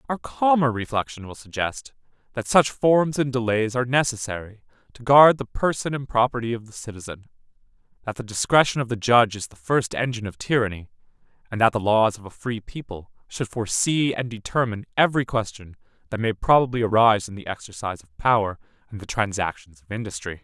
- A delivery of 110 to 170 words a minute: No, average, 180 wpm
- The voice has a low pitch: Yes, low, 115 Hz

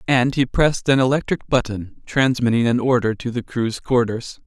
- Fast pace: No, average, 175 wpm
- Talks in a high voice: No, low, 125 Hz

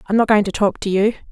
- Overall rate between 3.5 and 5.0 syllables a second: No, 6.7 syllables/s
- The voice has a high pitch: Yes, high, 205 Hz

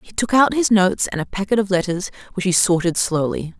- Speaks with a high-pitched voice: Yes, high, 195 Hz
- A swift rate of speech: Yes, fast, 235 wpm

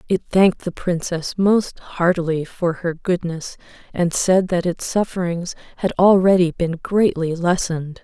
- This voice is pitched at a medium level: Yes, medium, 175 Hz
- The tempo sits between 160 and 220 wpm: No, average, 140 wpm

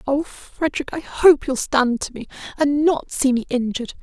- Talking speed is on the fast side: No, average, 195 wpm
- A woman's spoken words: Yes, female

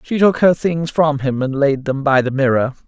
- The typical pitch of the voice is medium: Yes, medium, 145 Hz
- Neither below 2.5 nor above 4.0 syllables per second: No, 4.8 syllables/s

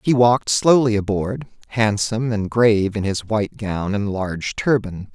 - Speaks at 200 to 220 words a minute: No, average, 165 wpm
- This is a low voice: Yes, low, 110 Hz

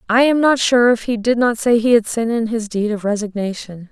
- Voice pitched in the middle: No, high, 225 Hz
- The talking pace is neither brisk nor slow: No, fast, 260 wpm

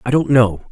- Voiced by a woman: No, male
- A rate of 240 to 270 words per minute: Yes, fast, 250 wpm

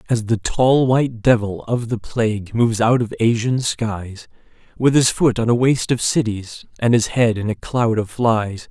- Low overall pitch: Yes, low, 115 Hz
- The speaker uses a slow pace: No, average, 200 wpm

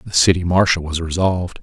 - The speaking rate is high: No, average, 185 wpm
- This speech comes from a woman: No, male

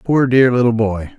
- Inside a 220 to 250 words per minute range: No, fast, 205 wpm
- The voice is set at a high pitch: No, low, 115 Hz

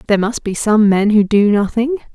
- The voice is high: Yes, high, 215 Hz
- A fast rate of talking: Yes, fast, 225 wpm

